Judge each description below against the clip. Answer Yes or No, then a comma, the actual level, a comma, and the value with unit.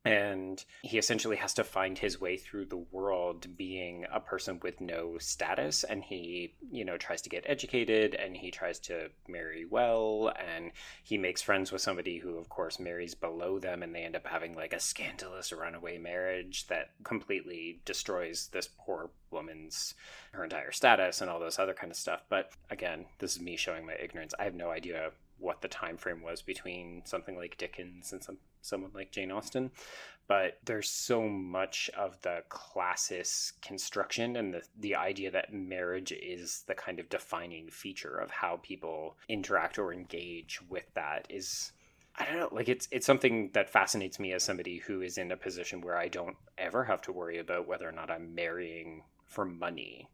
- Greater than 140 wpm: Yes, average, 190 wpm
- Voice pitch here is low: Yes, very low, 90 Hz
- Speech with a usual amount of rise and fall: No, narrow, 2.2 semitones